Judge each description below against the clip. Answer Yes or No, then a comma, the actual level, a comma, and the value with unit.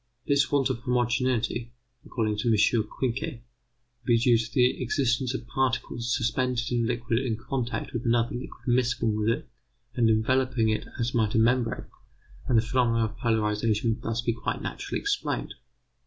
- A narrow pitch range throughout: Yes, narrow, 1.9 semitones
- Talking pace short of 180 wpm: Yes, average, 170 wpm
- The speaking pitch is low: Yes, low, 120 Hz